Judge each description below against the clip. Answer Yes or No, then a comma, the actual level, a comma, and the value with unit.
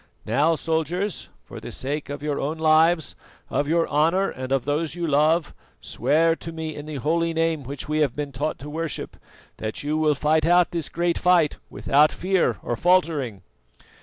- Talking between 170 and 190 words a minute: Yes, average, 185 wpm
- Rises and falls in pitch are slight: Yes, narrow, 2.3 semitones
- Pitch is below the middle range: No, medium, 155 Hz